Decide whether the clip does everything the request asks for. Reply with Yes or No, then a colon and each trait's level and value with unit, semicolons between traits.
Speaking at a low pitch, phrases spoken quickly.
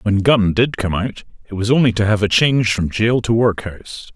Yes: low, 110 Hz; fast, 230 wpm